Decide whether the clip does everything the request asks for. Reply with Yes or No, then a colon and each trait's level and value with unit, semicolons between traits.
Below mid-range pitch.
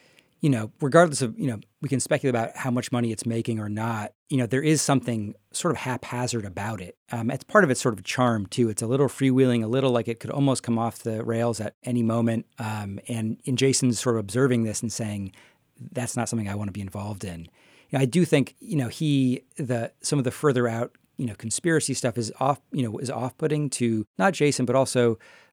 Yes: low, 125 Hz